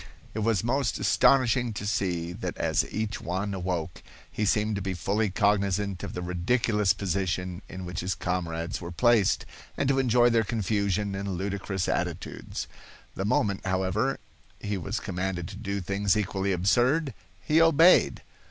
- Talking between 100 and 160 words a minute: Yes, average, 155 wpm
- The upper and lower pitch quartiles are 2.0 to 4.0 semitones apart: Yes, average, 3.0 semitones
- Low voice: Yes, low, 100 Hz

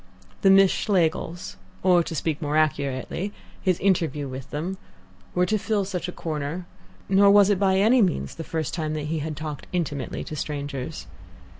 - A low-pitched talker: No, medium, 165 Hz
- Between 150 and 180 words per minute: Yes, average, 175 wpm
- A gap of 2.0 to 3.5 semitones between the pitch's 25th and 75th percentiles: No, average, 4.3 semitones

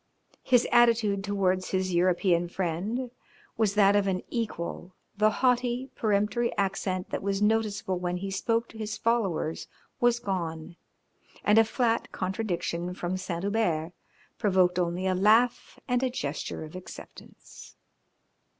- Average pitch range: Yes, average, 3.8 semitones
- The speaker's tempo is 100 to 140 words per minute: Yes, slow, 135 wpm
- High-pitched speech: Yes, high, 200 Hz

